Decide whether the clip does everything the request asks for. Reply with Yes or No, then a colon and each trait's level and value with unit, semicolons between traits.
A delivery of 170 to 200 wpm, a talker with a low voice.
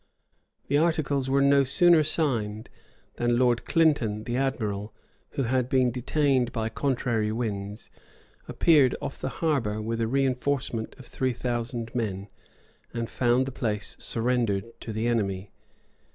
No: average, 140 wpm; low, 120 Hz